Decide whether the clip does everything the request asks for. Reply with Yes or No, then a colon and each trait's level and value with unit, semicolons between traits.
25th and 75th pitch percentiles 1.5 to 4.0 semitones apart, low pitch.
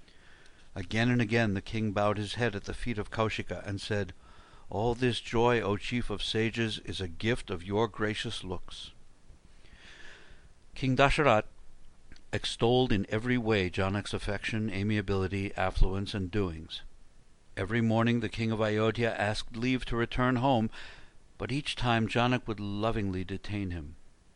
Yes: average, 3.2 semitones; low, 105 Hz